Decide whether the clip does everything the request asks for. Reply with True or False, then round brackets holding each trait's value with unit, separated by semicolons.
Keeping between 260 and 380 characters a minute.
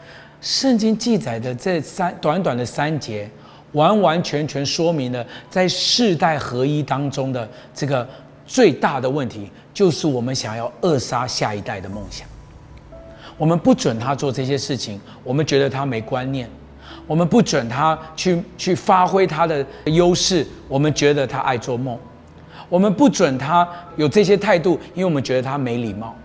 False (245 characters per minute)